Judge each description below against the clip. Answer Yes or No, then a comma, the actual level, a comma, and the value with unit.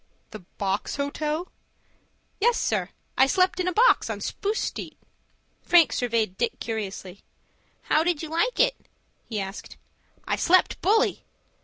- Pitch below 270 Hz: No, very high, 310 Hz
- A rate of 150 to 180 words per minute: No, average, 140 wpm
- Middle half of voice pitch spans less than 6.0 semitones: No, wide, 8.9 semitones